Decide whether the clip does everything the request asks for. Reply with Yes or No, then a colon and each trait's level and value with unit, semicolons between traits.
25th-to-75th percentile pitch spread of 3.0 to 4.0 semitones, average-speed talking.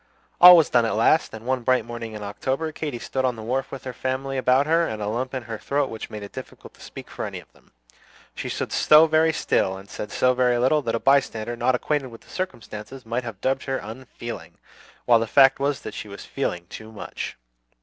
No: average, 3.3 semitones; fast, 235 wpm